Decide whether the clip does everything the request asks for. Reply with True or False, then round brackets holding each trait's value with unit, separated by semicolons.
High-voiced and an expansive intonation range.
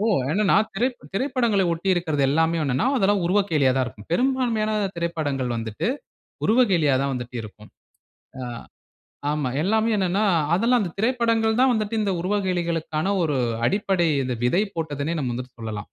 False (175 Hz; 6.8 semitones)